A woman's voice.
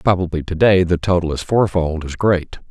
No: male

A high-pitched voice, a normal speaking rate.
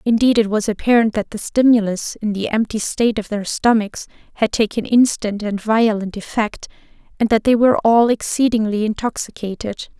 Yes: high, 220 Hz; average, 160 wpm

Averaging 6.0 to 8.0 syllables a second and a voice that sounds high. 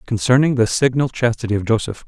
No: 6.2 syllables/s; low, 120 Hz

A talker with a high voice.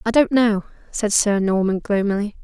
Yes: high, 215 Hz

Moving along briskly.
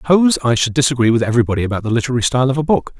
Yes: fast, 260 wpm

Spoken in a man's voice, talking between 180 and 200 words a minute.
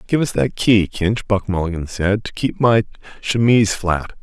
Yes: male; average, 185 wpm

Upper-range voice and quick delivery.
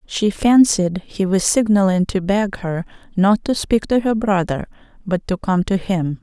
No: high, 195 Hz; average, 185 wpm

